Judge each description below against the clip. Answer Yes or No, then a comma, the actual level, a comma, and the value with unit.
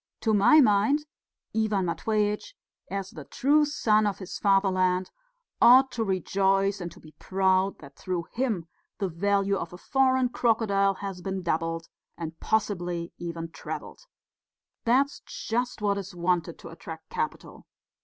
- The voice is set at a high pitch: Yes, high, 195 Hz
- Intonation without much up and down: No, average, 3.7 semitones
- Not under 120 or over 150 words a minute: Yes, average, 145 wpm